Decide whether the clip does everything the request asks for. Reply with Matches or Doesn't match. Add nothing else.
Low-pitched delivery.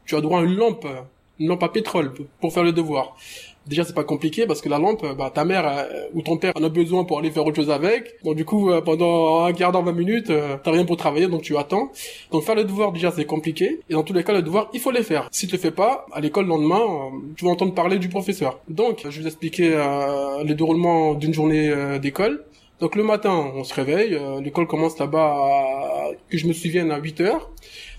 Doesn't match